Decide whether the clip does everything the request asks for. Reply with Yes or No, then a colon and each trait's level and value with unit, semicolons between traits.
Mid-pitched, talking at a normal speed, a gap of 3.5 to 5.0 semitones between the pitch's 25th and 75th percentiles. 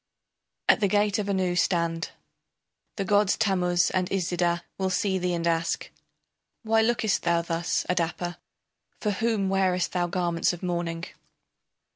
No: medium, 180 Hz; average, 145 wpm; narrow, 2.4 semitones